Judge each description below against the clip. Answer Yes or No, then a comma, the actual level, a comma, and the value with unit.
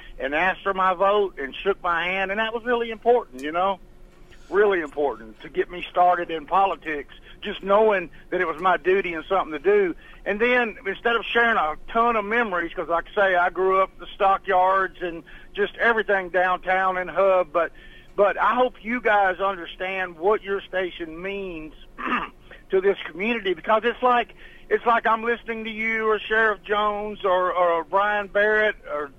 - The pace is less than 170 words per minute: No, average, 185 wpm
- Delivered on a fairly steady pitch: No, average, 3.8 semitones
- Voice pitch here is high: Yes, high, 195 Hz